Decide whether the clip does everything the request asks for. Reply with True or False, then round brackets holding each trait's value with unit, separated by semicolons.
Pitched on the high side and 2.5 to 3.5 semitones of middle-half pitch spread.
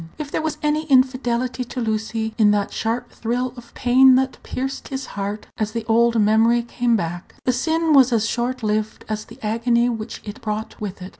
True (235 Hz; 2.9 semitones)